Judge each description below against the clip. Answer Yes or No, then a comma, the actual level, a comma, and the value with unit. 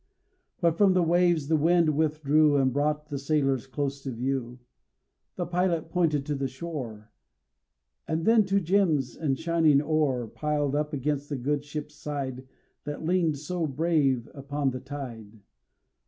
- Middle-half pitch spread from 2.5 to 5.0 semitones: Yes, average, 3.0 semitones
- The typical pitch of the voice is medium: Yes, medium, 150 Hz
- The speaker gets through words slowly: No, average, 155 wpm